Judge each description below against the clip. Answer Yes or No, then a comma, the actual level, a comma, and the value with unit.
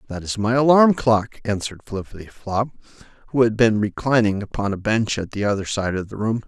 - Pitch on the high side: No, low, 110 Hz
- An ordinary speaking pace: Yes, average, 195 wpm